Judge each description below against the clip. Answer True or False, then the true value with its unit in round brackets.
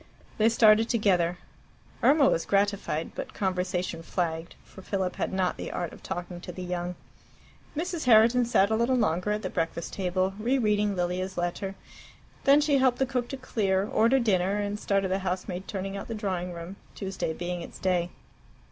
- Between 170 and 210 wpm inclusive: True (180 wpm)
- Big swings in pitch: False (3.6 semitones)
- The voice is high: True (195 Hz)